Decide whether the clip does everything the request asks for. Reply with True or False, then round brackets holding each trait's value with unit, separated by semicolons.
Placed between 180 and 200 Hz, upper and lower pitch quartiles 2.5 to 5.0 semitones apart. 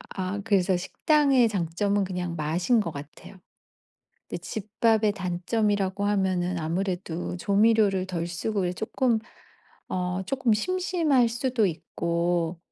True (195 Hz; 3.9 semitones)